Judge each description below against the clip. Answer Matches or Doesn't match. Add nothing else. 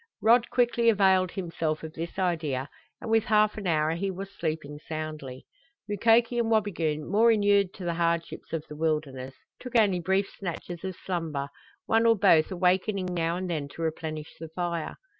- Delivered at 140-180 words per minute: Matches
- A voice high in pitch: Doesn't match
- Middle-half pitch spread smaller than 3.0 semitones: Doesn't match